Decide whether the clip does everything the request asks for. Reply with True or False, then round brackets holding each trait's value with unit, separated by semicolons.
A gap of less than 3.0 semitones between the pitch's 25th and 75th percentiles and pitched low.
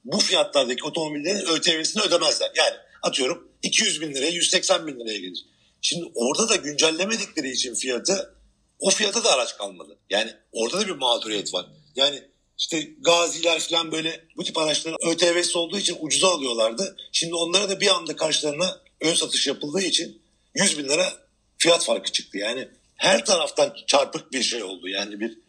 False (2.5 semitones; 165 Hz)